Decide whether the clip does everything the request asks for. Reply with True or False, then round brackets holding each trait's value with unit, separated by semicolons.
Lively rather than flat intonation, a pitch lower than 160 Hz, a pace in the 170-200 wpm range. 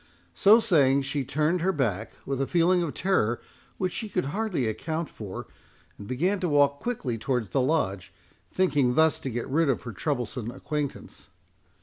True (5.7 semitones; 140 Hz; 175 wpm)